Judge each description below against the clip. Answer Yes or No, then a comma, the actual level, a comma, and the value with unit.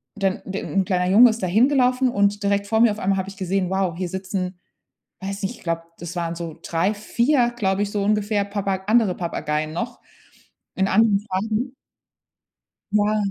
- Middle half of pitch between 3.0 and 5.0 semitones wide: No, narrow, 2.5 semitones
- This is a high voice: Yes, high, 200 Hz